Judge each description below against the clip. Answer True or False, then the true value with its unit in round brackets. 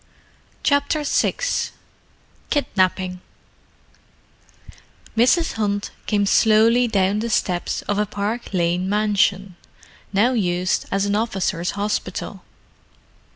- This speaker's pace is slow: True (95 wpm)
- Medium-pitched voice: False (205 Hz)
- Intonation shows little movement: False (3.2 semitones)